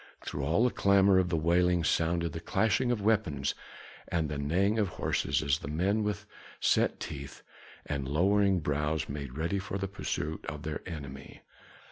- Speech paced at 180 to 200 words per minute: No, average, 170 wpm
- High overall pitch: No, very low, 85 Hz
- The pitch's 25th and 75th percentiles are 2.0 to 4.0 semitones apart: No, average, 5.1 semitones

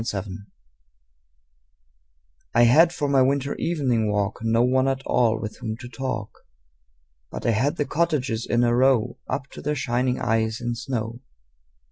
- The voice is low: Yes, low, 120 Hz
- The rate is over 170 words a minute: No, average, 160 wpm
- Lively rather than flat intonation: No, average, 3.1 semitones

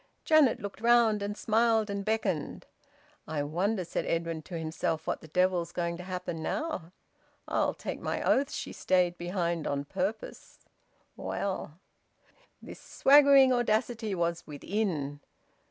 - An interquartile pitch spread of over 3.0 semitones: Yes, average, 4.8 semitones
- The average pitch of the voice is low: No, medium, 185 Hz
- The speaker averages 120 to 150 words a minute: Yes, average, 140 wpm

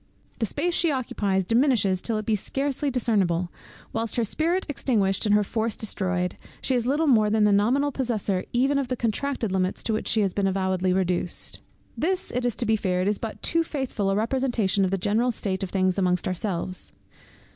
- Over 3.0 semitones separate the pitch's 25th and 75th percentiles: Yes, average, 4.8 semitones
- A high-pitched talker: Yes, high, 215 Hz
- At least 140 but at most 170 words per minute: No, average, 200 wpm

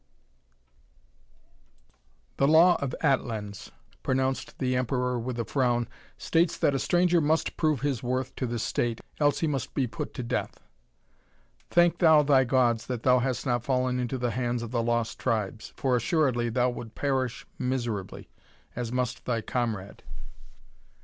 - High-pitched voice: No, low, 125 Hz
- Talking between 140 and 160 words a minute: Yes, average, 155 wpm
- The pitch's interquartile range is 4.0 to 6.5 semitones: No, narrow, 2.5 semitones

